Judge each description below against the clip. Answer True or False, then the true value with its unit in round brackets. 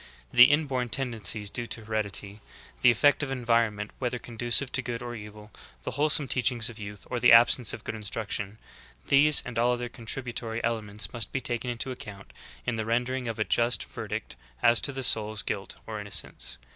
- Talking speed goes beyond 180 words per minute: True (195 wpm)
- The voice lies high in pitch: False (115 Hz)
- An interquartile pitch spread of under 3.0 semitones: True (2.5 semitones)